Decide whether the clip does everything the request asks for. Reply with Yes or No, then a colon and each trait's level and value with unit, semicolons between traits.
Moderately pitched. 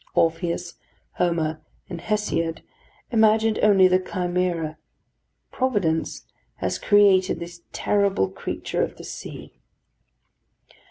Yes: medium, 180 Hz